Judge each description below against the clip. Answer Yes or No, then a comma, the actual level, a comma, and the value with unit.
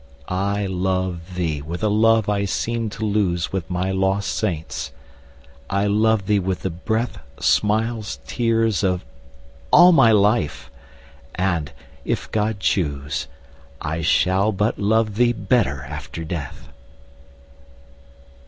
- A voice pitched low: Yes, low, 100 Hz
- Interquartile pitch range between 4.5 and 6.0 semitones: No, average, 3.8 semitones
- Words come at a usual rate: No, slow, 125 wpm